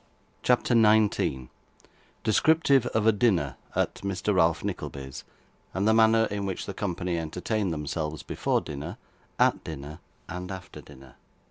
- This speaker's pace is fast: No, average, 140 wpm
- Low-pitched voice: Yes, very low, 95 Hz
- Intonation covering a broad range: Yes, wide, 6.0 semitones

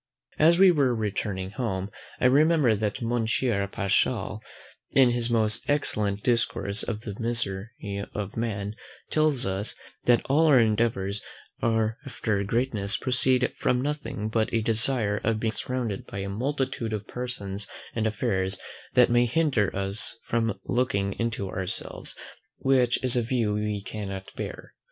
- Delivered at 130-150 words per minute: Yes, average, 140 wpm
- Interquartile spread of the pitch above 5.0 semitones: No, average, 3.7 semitones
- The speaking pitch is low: Yes, low, 115 Hz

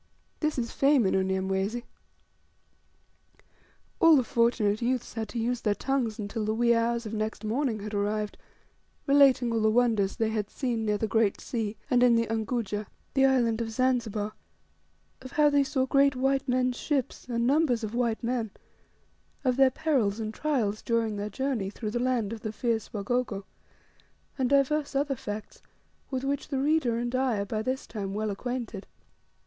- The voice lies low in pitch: No, high, 235 Hz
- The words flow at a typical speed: Yes, average, 175 wpm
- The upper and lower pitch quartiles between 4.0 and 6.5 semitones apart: No, average, 3.3 semitones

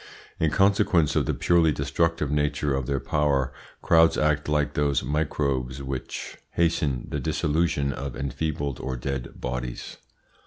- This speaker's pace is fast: No, average, 140 wpm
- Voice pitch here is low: Yes, very low, 70 Hz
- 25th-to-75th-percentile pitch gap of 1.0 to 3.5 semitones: Yes, narrow, 2.6 semitones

